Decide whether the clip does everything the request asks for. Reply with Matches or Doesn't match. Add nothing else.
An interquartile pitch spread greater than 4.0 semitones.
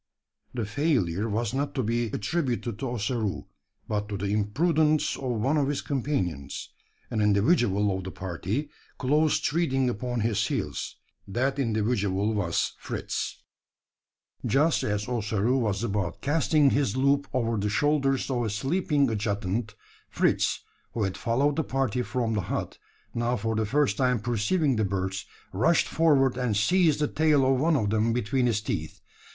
Matches